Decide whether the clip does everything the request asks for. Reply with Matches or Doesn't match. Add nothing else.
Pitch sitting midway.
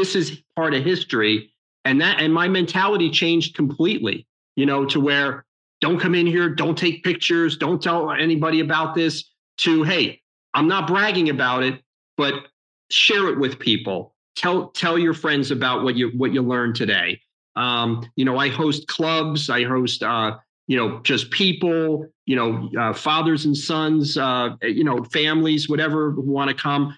Matches